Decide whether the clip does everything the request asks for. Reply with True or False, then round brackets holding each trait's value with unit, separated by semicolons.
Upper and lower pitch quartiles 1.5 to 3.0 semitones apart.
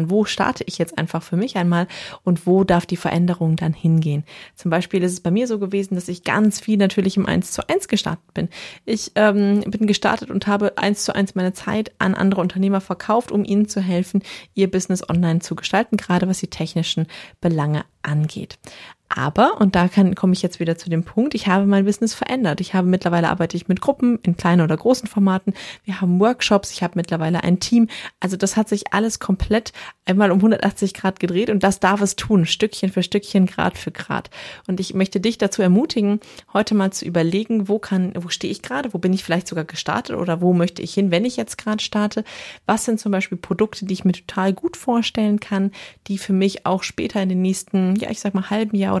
True (2.6 semitones)